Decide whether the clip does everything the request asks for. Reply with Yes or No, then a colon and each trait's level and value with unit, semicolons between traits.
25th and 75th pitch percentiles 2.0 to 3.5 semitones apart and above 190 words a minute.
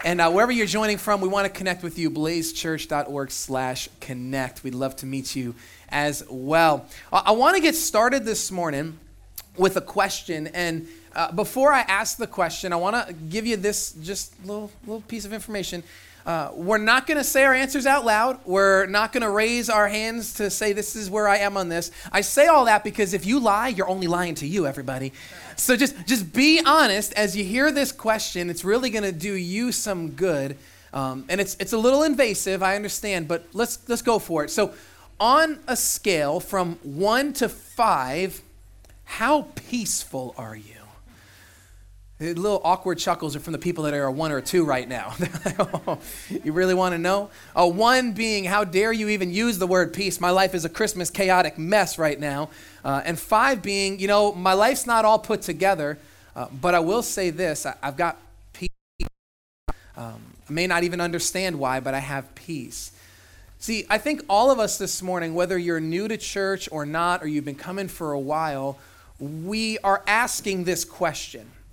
No: wide, 5.6 semitones; average, 200 wpm